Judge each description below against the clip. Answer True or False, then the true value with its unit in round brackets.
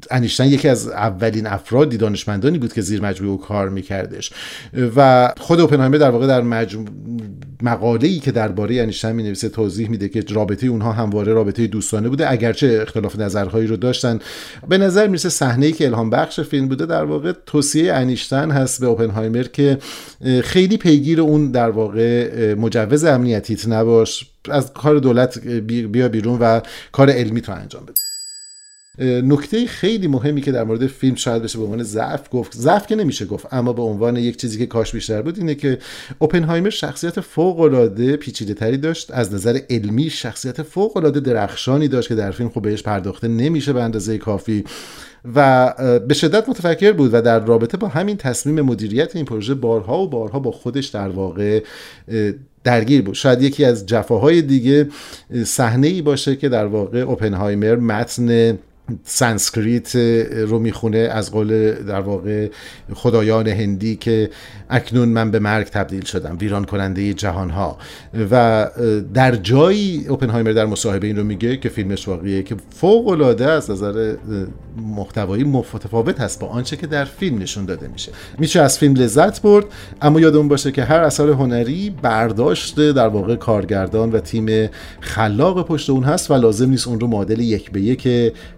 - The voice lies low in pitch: True (120 Hz)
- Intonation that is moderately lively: True (4.4 semitones)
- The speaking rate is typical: False (165 wpm)